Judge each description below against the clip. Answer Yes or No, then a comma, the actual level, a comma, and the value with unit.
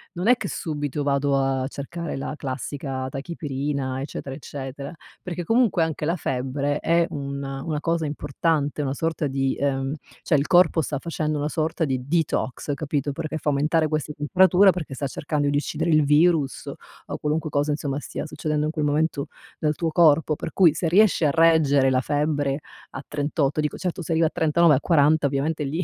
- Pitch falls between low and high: Yes, medium, 150 Hz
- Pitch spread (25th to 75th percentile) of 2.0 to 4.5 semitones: Yes, narrow, 2.6 semitones